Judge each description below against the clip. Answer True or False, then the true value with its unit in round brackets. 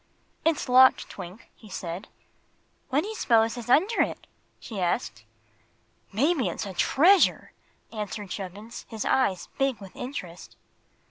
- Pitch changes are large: True (5.9 semitones)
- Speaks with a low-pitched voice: False (225 Hz)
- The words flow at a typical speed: False (130 wpm)